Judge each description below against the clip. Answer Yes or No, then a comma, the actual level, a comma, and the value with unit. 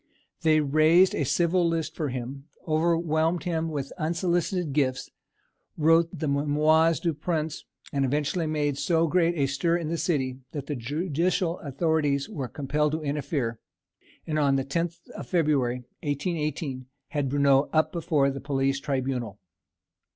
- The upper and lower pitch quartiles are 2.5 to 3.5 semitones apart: Yes, average, 3.1 semitones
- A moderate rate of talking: Yes, average, 145 wpm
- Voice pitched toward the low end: No, medium, 150 Hz